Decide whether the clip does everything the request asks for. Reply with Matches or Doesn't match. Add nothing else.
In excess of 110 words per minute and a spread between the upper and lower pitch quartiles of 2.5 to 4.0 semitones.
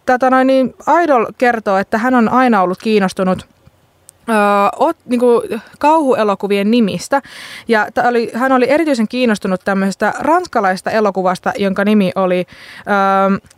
Doesn't match